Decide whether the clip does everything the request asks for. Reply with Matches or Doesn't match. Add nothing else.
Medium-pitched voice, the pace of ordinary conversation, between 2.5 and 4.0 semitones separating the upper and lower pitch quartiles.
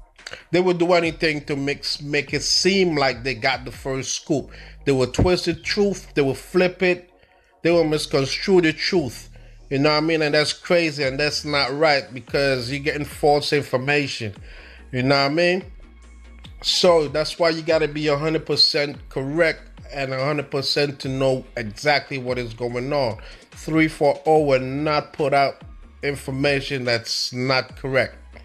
Matches